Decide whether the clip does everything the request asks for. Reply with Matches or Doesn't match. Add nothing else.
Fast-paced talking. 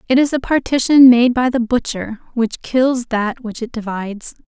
Doesn't match